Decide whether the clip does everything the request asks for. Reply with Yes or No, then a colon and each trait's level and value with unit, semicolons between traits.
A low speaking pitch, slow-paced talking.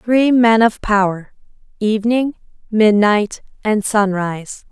No: high, 215 Hz; slow, 100 wpm